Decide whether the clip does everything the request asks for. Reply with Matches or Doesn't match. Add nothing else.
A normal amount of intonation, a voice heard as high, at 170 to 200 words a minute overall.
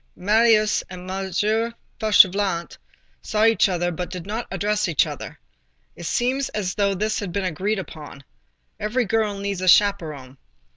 Doesn't match